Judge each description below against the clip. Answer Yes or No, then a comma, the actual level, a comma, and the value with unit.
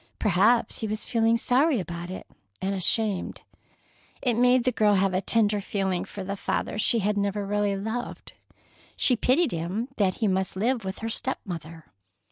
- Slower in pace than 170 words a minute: No, average, 175 wpm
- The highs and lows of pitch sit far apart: No, average, 3.4 semitones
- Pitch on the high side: Yes, high, 205 Hz